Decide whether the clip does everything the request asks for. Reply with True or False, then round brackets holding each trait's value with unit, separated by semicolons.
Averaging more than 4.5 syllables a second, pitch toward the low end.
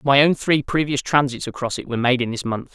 True (6.0 syllables/s; 130 Hz)